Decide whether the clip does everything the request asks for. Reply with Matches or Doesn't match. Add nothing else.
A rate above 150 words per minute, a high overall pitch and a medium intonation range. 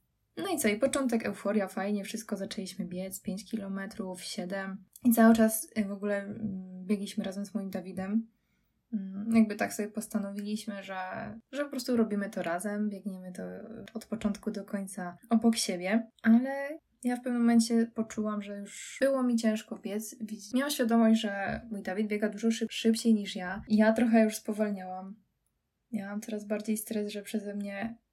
Doesn't match